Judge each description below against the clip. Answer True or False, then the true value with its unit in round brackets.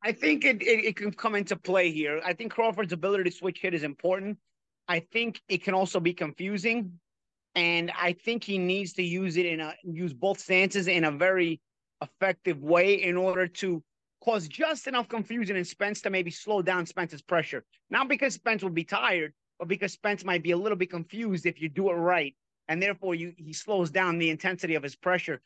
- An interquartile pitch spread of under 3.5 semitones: True (2.9 semitones)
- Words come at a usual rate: False (210 wpm)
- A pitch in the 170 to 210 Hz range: True (185 Hz)